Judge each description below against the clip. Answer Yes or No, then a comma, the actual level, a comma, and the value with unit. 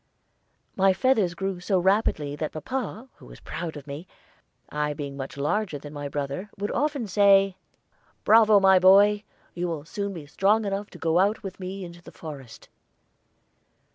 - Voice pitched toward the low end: No, medium, 185 Hz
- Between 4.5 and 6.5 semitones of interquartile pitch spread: Yes, average, 5.3 semitones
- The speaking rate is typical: Yes, average, 170 wpm